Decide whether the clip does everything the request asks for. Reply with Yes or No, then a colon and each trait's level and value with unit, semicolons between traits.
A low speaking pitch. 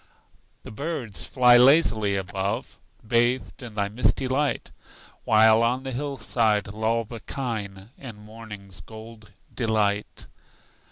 Yes: low, 110 Hz